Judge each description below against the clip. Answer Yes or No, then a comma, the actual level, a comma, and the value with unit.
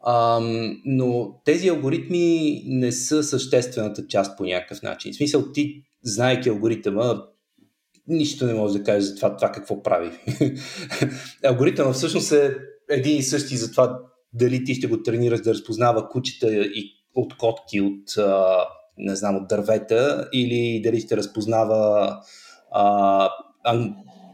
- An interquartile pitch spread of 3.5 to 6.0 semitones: Yes, average, 4.0 semitones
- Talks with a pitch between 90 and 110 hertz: No, low, 120 Hz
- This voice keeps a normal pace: Yes, average, 135 wpm